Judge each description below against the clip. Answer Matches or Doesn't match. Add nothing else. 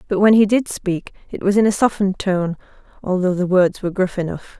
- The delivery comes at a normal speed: Doesn't match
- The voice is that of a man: Doesn't match